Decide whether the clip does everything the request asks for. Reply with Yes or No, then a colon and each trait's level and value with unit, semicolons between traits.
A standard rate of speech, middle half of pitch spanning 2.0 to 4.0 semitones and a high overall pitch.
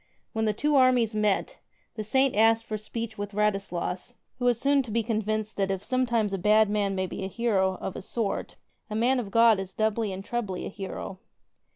No: fast, 220 wpm; average, 2.9 semitones; high, 215 Hz